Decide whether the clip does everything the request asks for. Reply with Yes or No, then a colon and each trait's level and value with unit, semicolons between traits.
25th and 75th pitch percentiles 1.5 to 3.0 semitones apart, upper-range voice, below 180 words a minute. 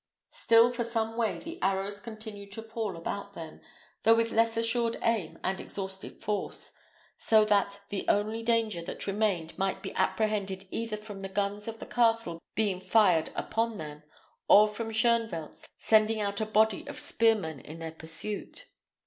Yes: average, 2.7 semitones; high, 210 Hz; average, 165 wpm